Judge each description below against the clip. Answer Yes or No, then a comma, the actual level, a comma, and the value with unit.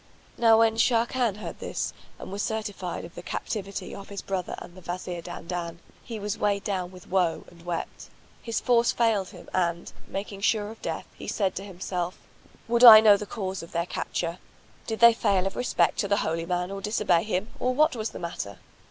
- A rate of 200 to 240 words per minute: Yes, fast, 205 wpm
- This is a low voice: No, high, 195 Hz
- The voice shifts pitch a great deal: No, average, 3.7 semitones